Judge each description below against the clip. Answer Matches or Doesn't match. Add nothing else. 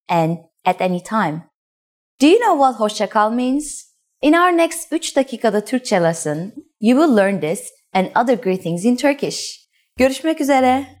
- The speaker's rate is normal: Matches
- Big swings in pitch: Matches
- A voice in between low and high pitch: Doesn't match